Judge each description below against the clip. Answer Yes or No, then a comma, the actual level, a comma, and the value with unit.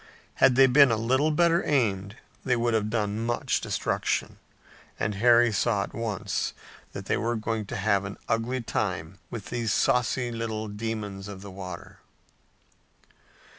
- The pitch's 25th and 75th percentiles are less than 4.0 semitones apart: Yes, average, 2.9 semitones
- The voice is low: Yes, low, 115 Hz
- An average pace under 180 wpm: Yes, average, 155 wpm